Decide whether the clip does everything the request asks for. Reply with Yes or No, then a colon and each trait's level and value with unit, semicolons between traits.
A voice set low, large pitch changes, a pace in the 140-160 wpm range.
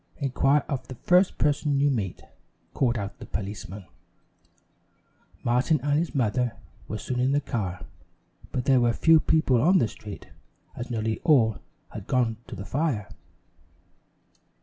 No: low, 125 Hz; average, 4.7 semitones; average, 150 wpm